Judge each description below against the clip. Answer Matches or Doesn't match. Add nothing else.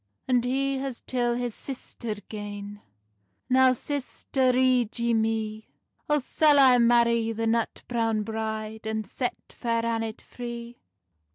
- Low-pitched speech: Doesn't match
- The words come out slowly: Matches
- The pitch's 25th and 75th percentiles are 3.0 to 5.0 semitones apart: Doesn't match